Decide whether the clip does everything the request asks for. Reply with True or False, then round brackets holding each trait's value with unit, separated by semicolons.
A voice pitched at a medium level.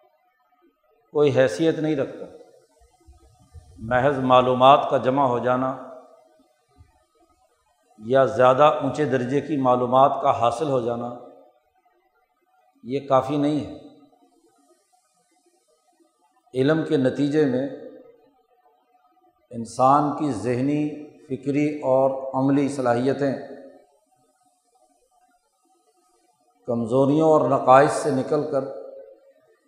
True (145 Hz)